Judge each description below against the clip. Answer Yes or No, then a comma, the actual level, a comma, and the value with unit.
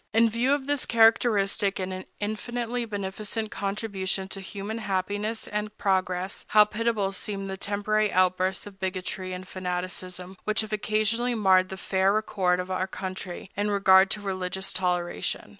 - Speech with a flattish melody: Yes, narrow, 2.3 semitones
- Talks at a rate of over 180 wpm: No, average, 150 wpm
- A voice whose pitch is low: No, high, 195 Hz